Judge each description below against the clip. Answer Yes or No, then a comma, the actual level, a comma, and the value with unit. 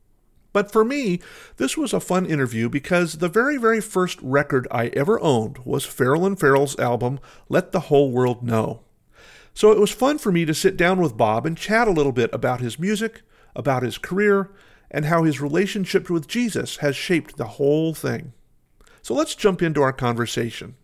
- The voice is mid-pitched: Yes, medium, 160 Hz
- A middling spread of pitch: No, wide, 6.7 semitones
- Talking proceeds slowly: No, average, 190 wpm